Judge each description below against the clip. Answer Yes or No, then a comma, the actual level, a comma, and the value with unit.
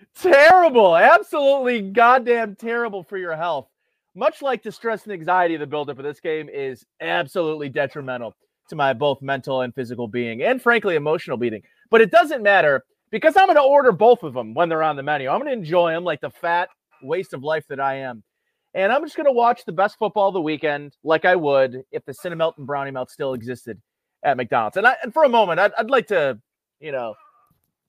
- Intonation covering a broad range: Yes, wide, 8.6 semitones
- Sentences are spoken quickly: Yes, fast, 215 wpm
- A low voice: No, medium, 175 Hz